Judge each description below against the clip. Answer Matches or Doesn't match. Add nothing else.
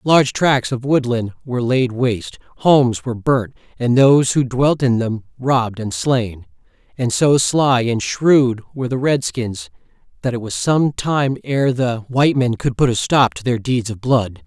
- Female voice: Doesn't match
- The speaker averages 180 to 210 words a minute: Matches